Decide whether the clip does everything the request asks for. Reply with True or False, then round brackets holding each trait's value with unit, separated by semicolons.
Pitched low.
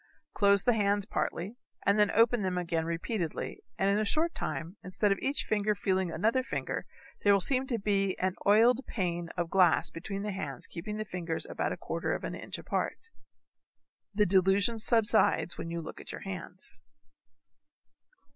False (200 Hz)